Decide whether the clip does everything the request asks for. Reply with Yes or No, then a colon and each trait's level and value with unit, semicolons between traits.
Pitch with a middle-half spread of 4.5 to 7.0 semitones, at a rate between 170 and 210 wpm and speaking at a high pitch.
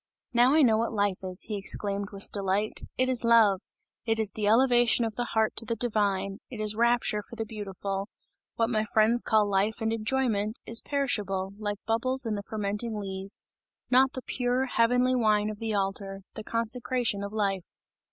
No: average, 2.8 semitones; average, 185 wpm; high, 215 Hz